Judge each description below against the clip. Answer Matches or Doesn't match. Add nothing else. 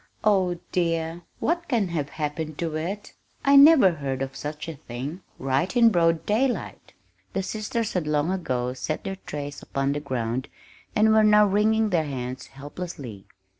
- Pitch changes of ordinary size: Doesn't match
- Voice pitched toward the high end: Doesn't match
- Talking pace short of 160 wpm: Doesn't match